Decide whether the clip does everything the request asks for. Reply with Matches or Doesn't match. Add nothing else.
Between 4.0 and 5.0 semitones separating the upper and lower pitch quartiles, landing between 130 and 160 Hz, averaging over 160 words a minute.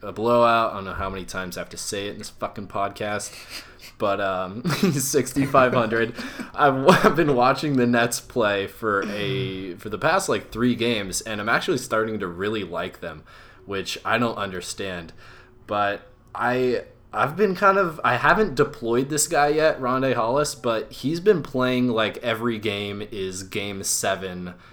Doesn't match